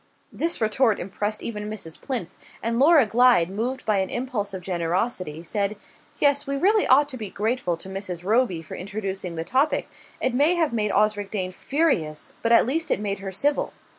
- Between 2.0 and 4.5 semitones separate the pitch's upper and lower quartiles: No, average, 5.3 semitones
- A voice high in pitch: Yes, high, 215 Hz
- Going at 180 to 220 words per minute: Yes, average, 190 wpm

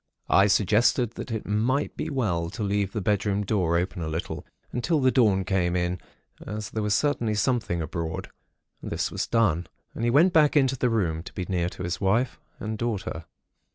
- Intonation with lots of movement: No, average, 4.8 semitones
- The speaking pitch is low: Yes, low, 105 Hz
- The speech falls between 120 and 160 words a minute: No, average, 190 wpm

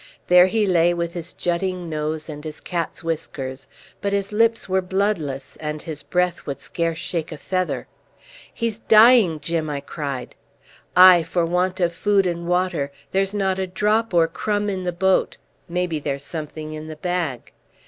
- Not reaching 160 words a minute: No, average, 170 wpm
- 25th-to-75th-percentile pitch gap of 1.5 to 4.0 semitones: Yes, average, 3.4 semitones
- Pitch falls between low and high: Yes, medium, 175 Hz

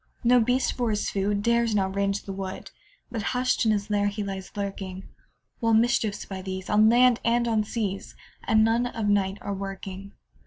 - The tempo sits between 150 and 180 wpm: No, average, 195 wpm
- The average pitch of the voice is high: Yes, high, 205 Hz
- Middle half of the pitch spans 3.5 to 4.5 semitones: No, average, 2.9 semitones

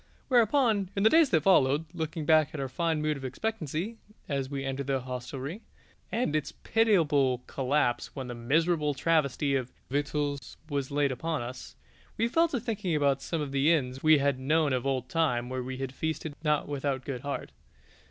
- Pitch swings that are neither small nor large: Yes, average, 3.6 semitones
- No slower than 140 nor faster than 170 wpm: No, average, 185 wpm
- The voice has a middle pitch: Yes, medium, 145 Hz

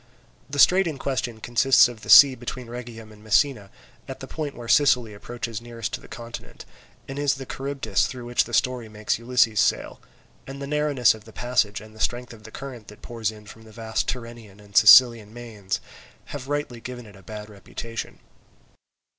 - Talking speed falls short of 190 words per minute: No, average, 195 wpm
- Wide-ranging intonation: No, average, 2.9 semitones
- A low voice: Yes, low, 120 Hz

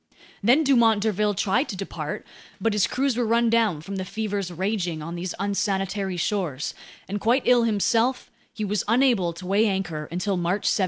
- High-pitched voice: Yes, high, 205 Hz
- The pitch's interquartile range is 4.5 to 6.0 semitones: No, average, 3.6 semitones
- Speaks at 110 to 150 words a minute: No, average, 180 wpm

